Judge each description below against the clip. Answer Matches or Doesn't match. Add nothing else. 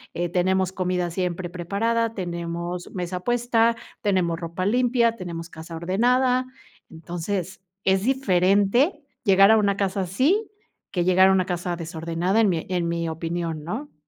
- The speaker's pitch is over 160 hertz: Matches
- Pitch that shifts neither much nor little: Matches